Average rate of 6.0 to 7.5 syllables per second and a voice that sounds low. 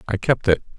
Yes: 6.1 syllables/s; low, 110 Hz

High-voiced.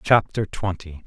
No: very low, 95 Hz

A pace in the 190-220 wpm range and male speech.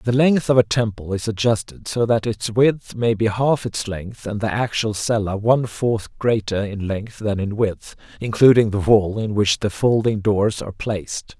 Yes: average, 200 wpm; male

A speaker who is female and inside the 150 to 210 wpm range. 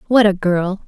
Yes: female; fast, 205 wpm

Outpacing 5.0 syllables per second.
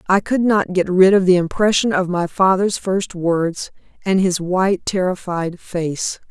No: 4.2 syllables/s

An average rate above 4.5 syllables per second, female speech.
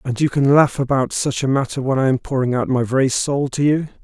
No: 5.8 syllables/s; male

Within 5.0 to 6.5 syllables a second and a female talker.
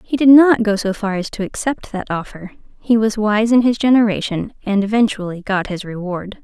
Yes: 5.2 syllables/s; female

